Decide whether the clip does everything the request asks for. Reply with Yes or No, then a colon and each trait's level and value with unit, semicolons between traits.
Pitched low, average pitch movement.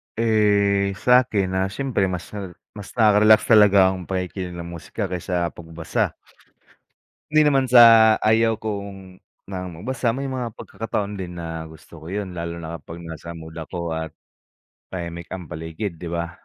Yes: very low, 95 Hz; average, 4.3 semitones